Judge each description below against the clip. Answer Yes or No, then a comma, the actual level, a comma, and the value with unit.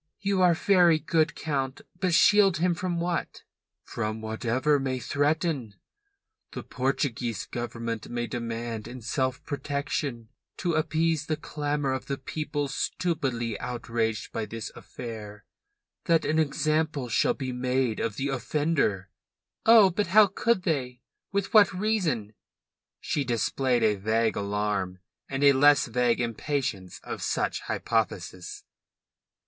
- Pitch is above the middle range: No, low, 135 Hz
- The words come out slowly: Yes, slow, 130 wpm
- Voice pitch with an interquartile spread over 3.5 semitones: Yes, wide, 5.6 semitones